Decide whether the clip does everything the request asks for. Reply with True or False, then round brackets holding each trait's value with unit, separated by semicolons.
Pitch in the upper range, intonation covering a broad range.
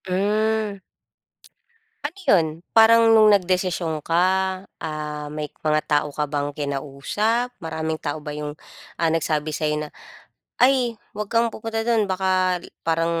False (170 Hz; 6.1 semitones)